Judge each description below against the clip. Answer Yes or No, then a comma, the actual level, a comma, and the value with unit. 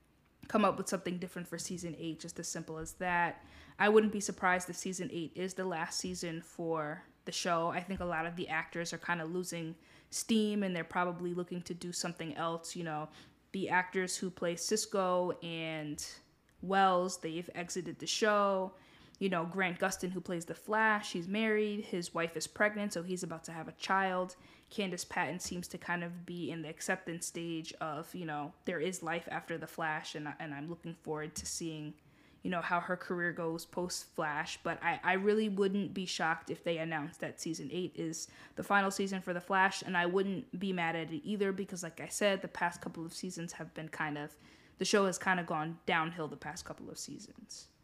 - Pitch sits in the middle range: Yes, medium, 175 Hz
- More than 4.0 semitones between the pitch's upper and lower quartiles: No, narrow, 2.5 semitones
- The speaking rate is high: Yes, fast, 210 wpm